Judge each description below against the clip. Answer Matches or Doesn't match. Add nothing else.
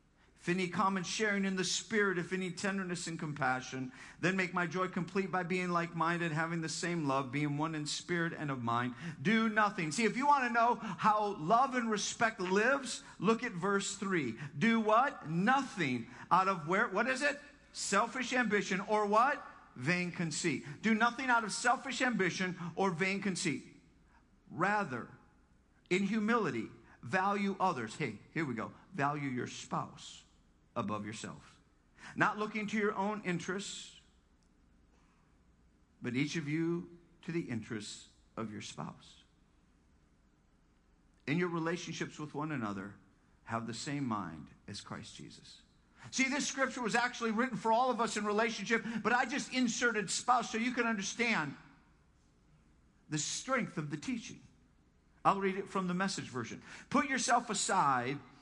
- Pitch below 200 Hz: Matches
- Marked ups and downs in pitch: Matches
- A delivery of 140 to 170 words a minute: Matches